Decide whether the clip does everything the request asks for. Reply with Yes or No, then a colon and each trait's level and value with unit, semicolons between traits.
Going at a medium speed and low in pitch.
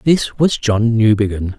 Yes: average, 150 wpm; low, 115 Hz